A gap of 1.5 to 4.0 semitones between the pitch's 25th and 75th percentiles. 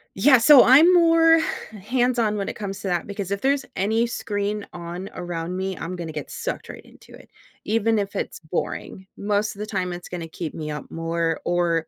No: average, 4.5 semitones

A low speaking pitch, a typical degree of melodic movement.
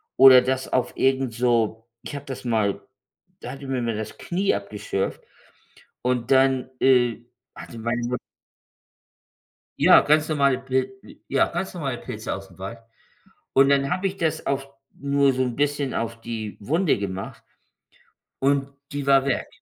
Yes: low, 130 Hz; average, 3.1 semitones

